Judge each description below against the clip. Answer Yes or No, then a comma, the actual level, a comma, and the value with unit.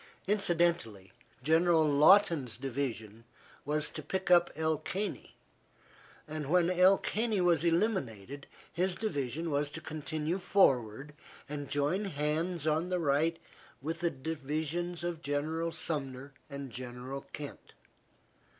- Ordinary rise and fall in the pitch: Yes, average, 3.7 semitones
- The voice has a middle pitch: Yes, medium, 155 Hz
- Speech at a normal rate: No, slow, 120 wpm